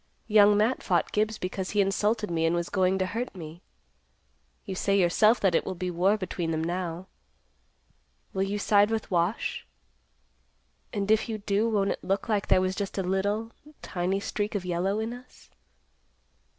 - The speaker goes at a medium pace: Yes, average, 175 wpm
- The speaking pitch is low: No, high, 195 Hz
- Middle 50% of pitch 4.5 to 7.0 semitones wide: No, narrow, 2.5 semitones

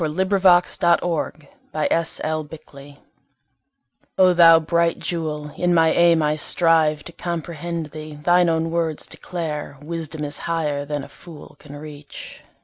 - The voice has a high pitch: No, medium, 160 Hz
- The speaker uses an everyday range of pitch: No, narrow, 2.2 semitones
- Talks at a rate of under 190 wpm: Yes, average, 140 wpm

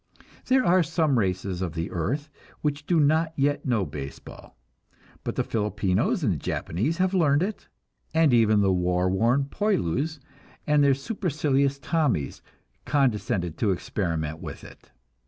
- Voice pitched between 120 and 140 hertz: Yes, low, 135 Hz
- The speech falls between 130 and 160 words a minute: Yes, average, 145 wpm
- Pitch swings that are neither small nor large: No, wide, 8.9 semitones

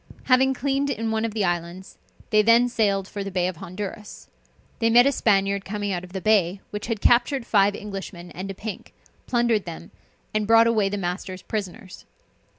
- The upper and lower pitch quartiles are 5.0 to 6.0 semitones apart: No, average, 3.1 semitones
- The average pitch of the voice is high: Yes, high, 205 Hz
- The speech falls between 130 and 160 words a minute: No, average, 190 wpm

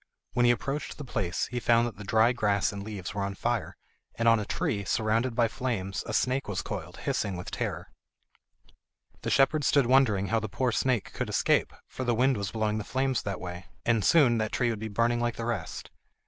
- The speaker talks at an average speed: No, fast, 220 wpm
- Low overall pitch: Yes, low, 115 Hz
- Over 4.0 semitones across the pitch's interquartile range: No, average, 3.3 semitones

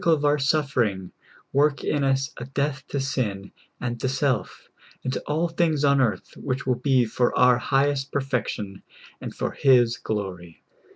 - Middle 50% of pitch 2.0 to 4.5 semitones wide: Yes, average, 2.9 semitones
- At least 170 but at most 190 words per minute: Yes, average, 175 wpm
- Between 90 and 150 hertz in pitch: Yes, low, 135 Hz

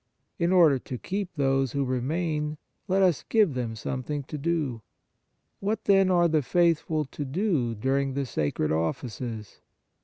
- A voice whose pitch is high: No, medium, 145 Hz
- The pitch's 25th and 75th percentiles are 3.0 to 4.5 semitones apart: No, average, 5.1 semitones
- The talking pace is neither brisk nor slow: Yes, average, 150 wpm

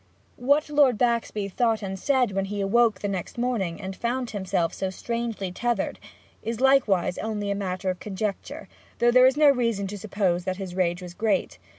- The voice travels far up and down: No, average, 3.9 semitones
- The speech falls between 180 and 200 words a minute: Yes, average, 185 wpm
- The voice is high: Yes, high, 205 Hz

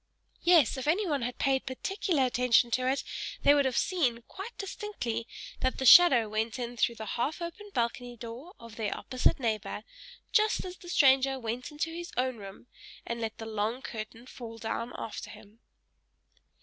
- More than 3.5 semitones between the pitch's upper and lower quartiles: Yes, average, 4.4 semitones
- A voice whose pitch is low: No, very high, 250 Hz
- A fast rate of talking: No, average, 175 wpm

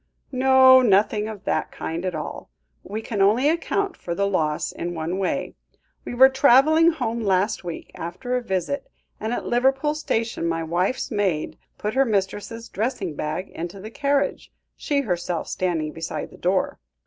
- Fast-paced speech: No, average, 165 wpm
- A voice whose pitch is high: Yes, high, 210 Hz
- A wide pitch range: Yes, wide, 6.7 semitones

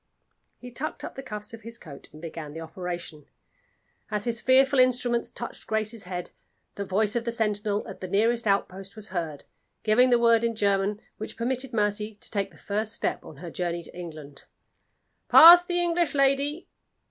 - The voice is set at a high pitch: Yes, high, 215 Hz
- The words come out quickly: No, average, 180 wpm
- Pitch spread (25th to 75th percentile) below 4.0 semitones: No, average, 4.4 semitones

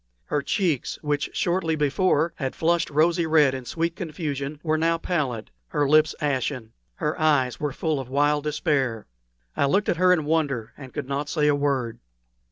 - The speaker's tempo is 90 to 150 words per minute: No, average, 180 wpm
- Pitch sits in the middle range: Yes, medium, 150 Hz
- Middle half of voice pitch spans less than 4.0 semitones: Yes, average, 2.8 semitones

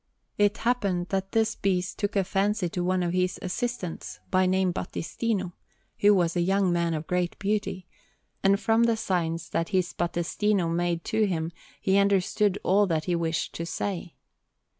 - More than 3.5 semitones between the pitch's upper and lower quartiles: No, average, 2.8 semitones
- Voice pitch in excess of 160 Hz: Yes, medium, 185 Hz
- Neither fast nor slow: Yes, average, 170 wpm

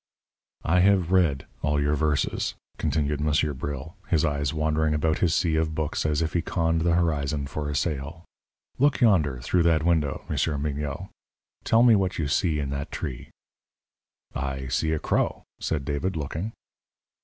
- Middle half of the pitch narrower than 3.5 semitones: Yes, narrow, 2.6 semitones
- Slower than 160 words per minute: No, average, 165 wpm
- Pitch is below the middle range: Yes, very low, 75 Hz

